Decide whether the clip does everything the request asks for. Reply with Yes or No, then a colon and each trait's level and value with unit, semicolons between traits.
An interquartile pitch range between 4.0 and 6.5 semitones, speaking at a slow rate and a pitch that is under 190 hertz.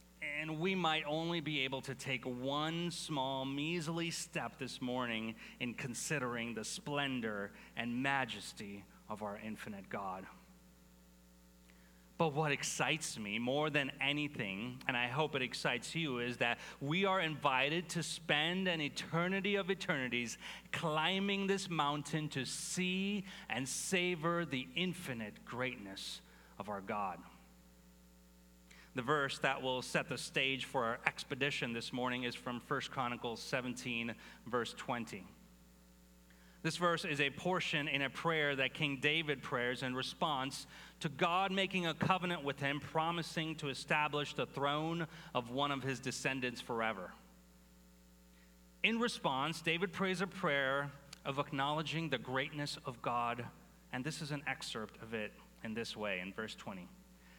No: average, 5.3 semitones; average, 145 wpm; medium, 140 Hz